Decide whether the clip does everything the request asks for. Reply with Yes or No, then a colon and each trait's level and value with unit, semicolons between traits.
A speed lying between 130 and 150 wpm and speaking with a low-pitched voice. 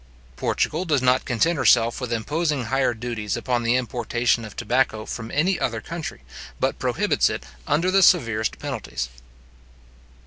Yes: average, 145 wpm; low, 125 Hz